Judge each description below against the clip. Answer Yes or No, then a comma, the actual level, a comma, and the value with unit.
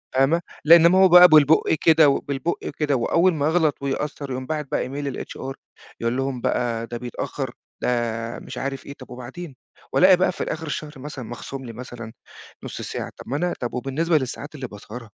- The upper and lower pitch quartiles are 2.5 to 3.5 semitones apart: No, average, 4.1 semitones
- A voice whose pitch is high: No, medium, 140 Hz